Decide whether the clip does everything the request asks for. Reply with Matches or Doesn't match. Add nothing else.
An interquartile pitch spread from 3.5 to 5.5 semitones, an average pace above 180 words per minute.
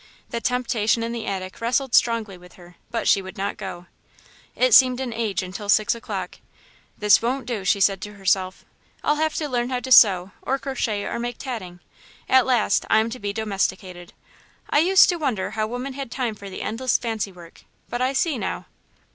Matches